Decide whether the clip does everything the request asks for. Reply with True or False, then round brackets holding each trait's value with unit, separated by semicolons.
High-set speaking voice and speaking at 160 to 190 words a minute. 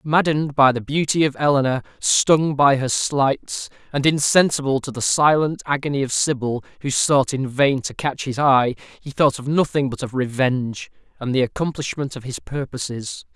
False (135 Hz; 175 wpm)